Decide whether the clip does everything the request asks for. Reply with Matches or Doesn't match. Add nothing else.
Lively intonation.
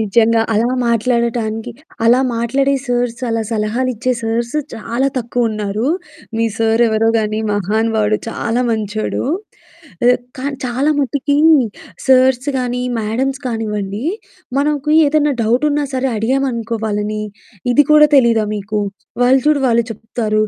Doesn't match